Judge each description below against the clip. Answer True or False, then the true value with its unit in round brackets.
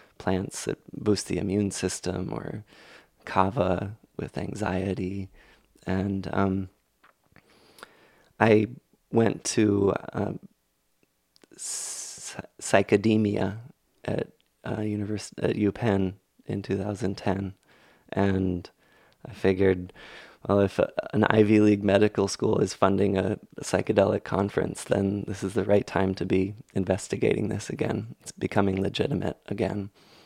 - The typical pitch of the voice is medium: False (100 Hz)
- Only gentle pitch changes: True (1.7 semitones)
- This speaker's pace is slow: True (115 wpm)